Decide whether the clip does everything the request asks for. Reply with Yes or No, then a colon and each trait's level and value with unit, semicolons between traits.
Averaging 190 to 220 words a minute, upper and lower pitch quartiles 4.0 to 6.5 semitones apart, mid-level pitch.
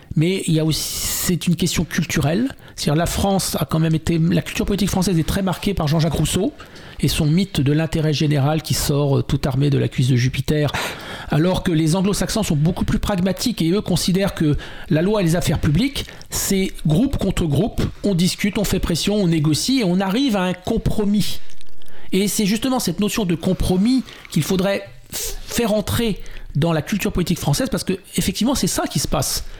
Yes: average, 205 wpm; average, 4.3 semitones; medium, 180 Hz